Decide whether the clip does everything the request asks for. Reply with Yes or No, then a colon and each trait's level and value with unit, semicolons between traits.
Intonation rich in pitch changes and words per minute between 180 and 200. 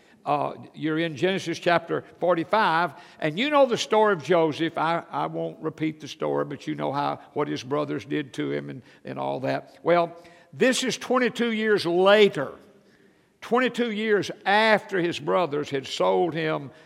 Yes: wide, 5.8 semitones; average, 185 wpm